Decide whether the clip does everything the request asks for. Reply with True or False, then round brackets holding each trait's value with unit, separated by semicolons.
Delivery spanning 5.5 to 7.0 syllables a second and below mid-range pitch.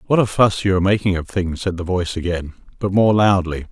True (6.1 syllables/s; 95 Hz)